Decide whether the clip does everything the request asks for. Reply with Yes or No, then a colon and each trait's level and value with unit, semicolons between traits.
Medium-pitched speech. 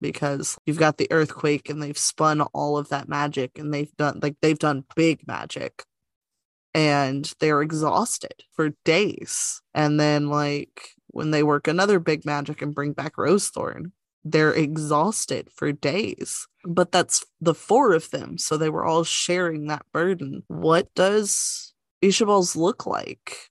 Yes: medium, 155 Hz